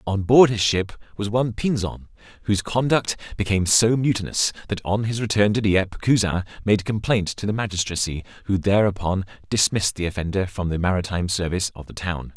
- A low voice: Yes, low, 100 Hz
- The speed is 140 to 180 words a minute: Yes, average, 175 wpm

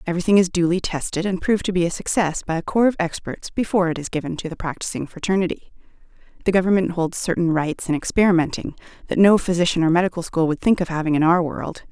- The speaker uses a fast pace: Yes, fast, 215 wpm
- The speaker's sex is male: No, female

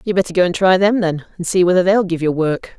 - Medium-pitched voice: Yes, medium, 180 Hz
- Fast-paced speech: Yes, fast, 300 wpm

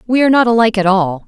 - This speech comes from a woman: Yes, female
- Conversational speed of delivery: No, fast, 285 wpm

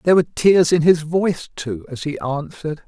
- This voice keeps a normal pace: No, fast, 210 wpm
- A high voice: No, medium, 160 Hz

